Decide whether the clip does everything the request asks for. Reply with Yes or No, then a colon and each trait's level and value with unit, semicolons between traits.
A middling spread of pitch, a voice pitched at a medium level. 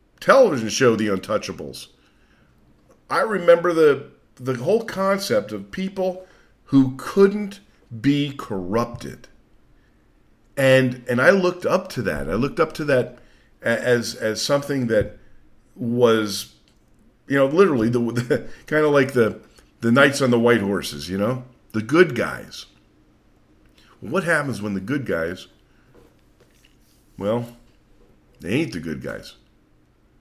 No: average, 4.9 semitones; low, 125 Hz